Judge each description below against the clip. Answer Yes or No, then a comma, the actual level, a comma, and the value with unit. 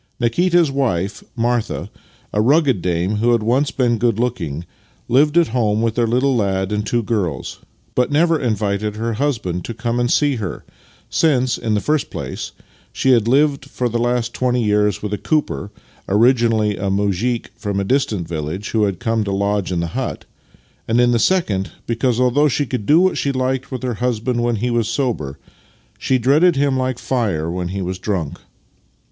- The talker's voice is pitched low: Yes, low, 115 Hz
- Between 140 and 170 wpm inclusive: No, average, 190 wpm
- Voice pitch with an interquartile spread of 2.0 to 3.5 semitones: No, average, 4.0 semitones